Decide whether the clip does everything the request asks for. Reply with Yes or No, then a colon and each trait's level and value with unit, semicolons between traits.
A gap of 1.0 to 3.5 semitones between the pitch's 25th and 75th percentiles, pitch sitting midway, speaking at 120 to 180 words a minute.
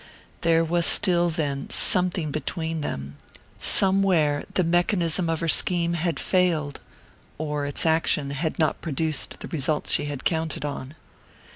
Yes: average, 2.7 semitones; medium, 160 Hz; average, 140 wpm